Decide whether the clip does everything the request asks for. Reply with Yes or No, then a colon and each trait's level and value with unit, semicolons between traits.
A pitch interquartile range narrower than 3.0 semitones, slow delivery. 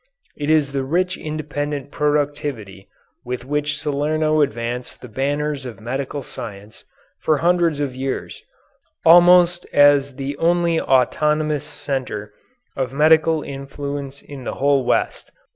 Yes: narrow, 2.5 semitones; slow, 125 wpm